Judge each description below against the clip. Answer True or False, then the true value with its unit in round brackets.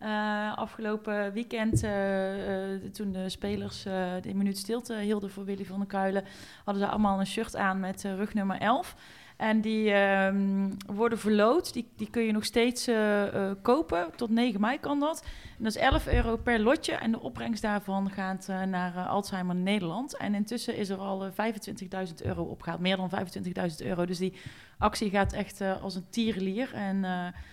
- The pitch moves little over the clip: True (2.3 semitones)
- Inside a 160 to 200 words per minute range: True (195 wpm)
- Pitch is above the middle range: True (200 Hz)